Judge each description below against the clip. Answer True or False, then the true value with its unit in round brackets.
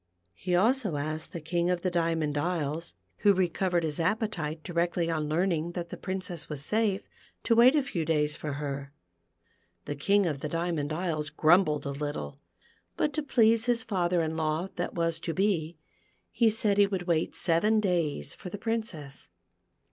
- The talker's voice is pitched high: False (170 Hz)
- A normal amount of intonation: True (4.1 semitones)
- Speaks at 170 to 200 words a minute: True (175 wpm)